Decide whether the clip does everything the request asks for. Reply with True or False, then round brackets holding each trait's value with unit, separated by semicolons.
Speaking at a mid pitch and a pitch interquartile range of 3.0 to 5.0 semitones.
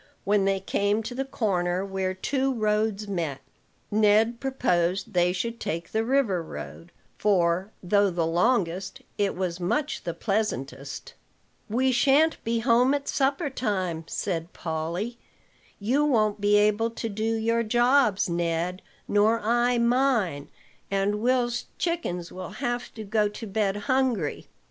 False (210 Hz; 4.6 semitones)